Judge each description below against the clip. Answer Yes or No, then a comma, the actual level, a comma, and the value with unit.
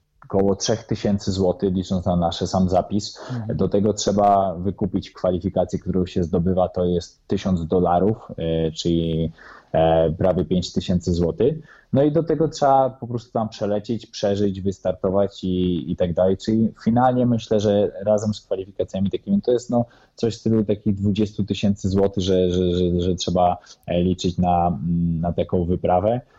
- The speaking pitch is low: Yes, very low, 95 Hz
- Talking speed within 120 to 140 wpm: No, average, 150 wpm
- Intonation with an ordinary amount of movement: Yes, average, 3.0 semitones